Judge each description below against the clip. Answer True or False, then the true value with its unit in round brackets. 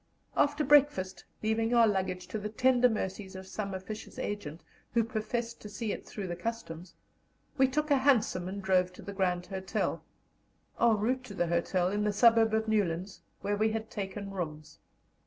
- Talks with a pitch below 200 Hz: False (205 Hz)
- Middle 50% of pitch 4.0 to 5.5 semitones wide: False (3.5 semitones)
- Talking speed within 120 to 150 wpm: False (180 wpm)